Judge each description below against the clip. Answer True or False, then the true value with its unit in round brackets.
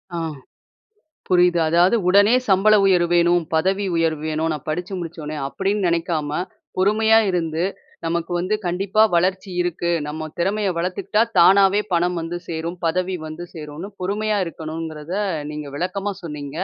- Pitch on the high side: False (175 Hz)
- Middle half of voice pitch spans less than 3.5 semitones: True (2.9 semitones)